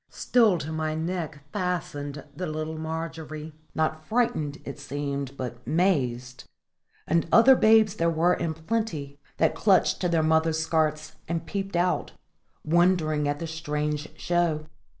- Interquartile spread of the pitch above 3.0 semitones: No, narrow, 2.5 semitones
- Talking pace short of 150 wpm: Yes, average, 140 wpm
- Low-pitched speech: No, medium, 160 Hz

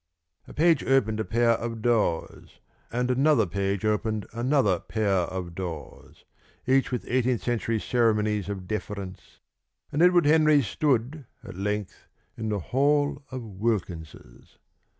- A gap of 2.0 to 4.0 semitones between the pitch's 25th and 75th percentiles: No, average, 4.4 semitones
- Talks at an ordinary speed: No, slow, 130 wpm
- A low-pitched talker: Yes, low, 115 Hz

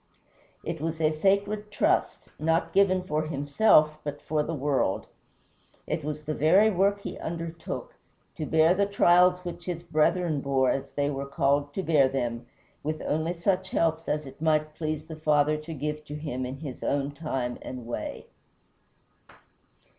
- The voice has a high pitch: No, medium, 155 Hz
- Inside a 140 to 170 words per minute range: Yes, average, 160 wpm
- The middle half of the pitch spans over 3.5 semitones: No, average, 3.0 semitones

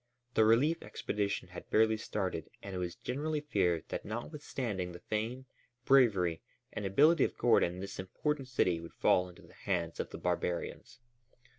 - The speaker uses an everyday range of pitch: No, wide, 6.0 semitones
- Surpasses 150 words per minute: Yes, average, 160 wpm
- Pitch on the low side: Yes, low, 105 Hz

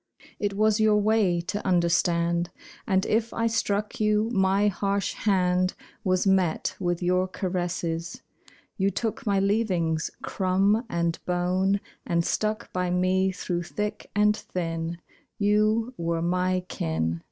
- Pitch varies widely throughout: No, average, 3.1 semitones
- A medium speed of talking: No, slow, 130 wpm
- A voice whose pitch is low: No, medium, 185 Hz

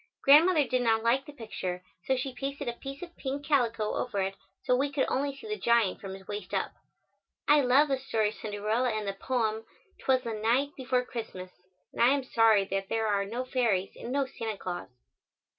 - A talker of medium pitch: No, high, 240 Hz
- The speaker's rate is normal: No, fast, 210 wpm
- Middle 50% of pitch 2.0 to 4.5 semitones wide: Yes, average, 4.2 semitones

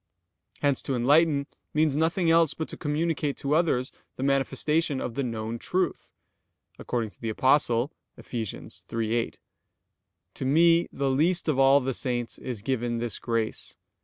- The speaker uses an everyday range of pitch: Yes, average, 4.5 semitones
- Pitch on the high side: No, low, 135 Hz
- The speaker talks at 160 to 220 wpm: No, average, 150 wpm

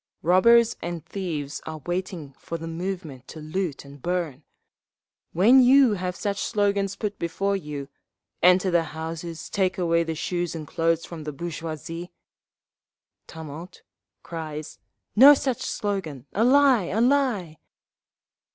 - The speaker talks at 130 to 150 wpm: Yes, slow, 135 wpm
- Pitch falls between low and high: Yes, medium, 175 Hz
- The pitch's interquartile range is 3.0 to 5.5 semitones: Yes, average, 3.9 semitones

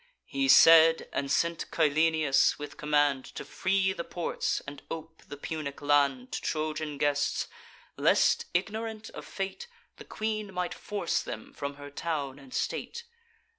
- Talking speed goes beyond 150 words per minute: No, average, 145 wpm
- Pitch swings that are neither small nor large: Yes, average, 4.5 semitones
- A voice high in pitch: No, medium, 155 Hz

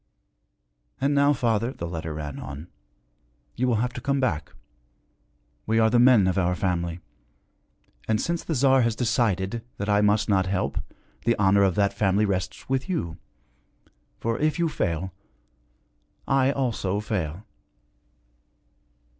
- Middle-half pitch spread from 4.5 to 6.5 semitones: Yes, average, 5.2 semitones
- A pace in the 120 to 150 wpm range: Yes, average, 145 wpm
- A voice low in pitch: Yes, low, 105 Hz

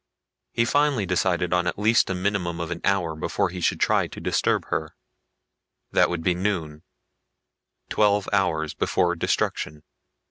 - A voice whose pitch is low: Yes, very low, 90 Hz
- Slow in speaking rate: No, average, 150 wpm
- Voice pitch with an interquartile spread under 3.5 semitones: Yes, average, 3.1 semitones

